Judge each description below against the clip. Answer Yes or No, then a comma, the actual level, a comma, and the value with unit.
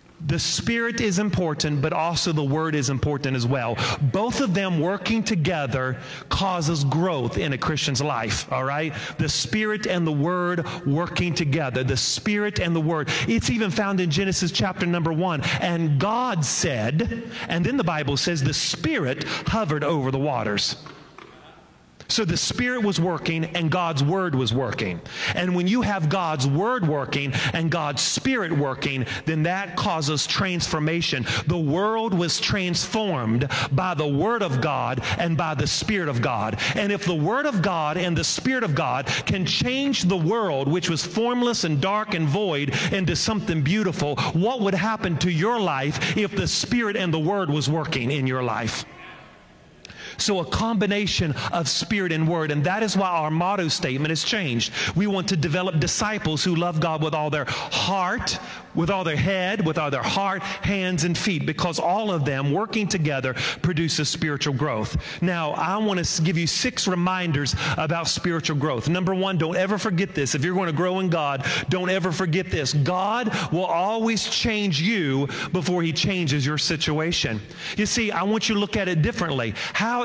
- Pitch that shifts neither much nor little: Yes, average, 4.6 semitones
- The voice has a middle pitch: Yes, medium, 165 Hz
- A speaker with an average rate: Yes, average, 180 wpm